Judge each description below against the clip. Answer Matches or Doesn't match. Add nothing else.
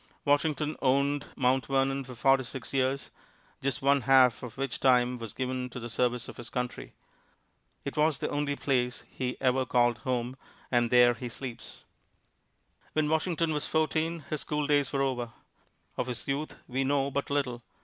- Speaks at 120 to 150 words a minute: Doesn't match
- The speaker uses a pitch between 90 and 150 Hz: Matches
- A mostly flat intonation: Matches